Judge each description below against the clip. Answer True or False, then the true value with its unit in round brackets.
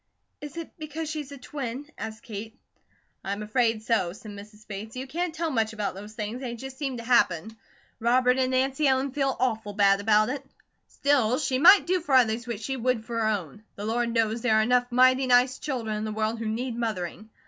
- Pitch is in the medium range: False (235 Hz)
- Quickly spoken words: True (215 wpm)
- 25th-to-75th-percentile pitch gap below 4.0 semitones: True (3.4 semitones)